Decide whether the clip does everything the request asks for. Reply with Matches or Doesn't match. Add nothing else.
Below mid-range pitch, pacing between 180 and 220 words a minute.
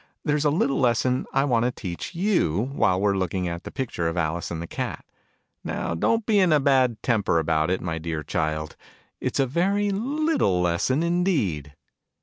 Matches